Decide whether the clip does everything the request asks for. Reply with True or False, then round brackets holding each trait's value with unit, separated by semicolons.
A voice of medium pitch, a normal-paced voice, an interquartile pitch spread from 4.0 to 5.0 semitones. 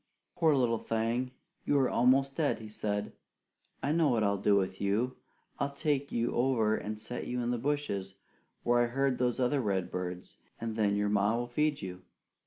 False (120 Hz; 190 wpm; 4.5 semitones)